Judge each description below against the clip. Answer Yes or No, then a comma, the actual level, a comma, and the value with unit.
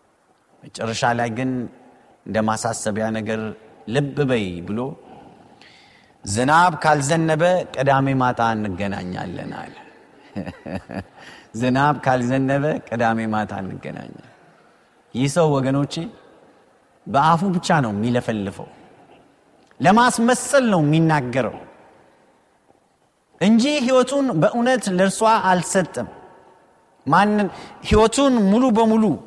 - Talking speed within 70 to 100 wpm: Yes, average, 80 wpm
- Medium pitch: Yes, medium, 145 Hz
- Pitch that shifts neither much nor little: No, wide, 8.7 semitones